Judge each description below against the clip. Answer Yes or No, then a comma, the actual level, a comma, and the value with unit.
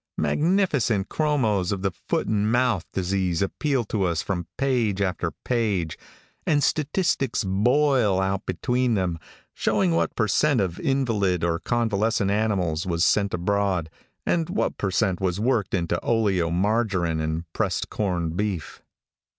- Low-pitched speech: Yes, low, 100 Hz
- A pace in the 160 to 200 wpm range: No, average, 140 wpm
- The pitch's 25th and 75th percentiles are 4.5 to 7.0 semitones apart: Yes, average, 4.9 semitones